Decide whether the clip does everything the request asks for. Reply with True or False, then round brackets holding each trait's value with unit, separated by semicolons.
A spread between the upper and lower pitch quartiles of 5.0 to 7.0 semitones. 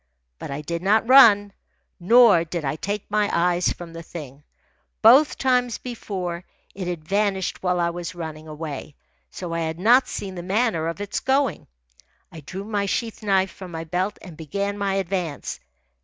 False (3.7 semitones)